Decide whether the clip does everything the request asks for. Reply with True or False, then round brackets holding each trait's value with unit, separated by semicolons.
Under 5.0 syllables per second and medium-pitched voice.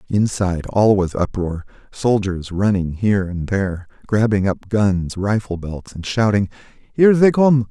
False (4.5 syllables/s; 100 Hz)